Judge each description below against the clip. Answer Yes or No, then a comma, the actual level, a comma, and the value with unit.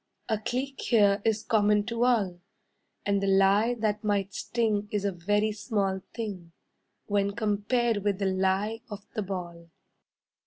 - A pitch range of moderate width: No, narrow, 2.2 semitones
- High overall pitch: Yes, high, 205 Hz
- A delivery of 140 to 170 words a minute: Yes, average, 150 wpm